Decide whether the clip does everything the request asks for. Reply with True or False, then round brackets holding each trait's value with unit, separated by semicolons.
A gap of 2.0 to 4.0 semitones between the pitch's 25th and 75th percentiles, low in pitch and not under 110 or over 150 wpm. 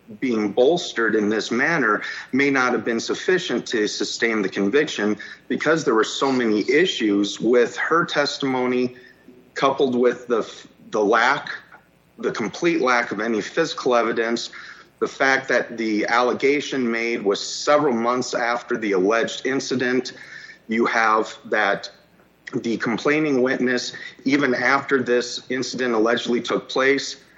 True (2.8 semitones; 125 Hz; 135 wpm)